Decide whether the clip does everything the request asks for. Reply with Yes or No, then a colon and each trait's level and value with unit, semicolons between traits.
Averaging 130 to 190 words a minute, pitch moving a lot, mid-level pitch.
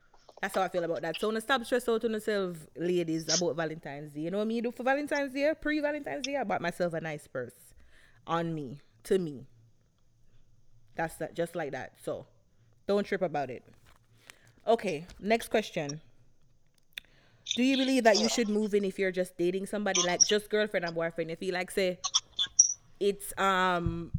Yes: average, 180 wpm; wide, 6.0 semitones; medium, 180 Hz